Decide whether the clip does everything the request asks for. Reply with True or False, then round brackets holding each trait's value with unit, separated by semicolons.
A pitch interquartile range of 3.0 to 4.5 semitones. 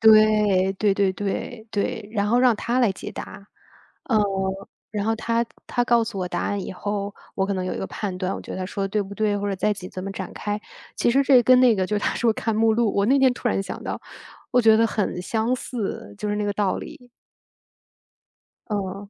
False (2.5 semitones)